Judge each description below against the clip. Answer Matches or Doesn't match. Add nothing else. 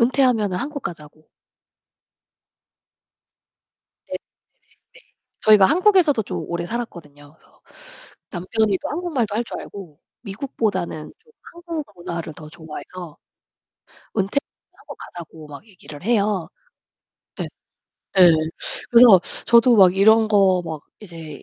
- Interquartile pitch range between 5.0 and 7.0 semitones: Matches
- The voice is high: Matches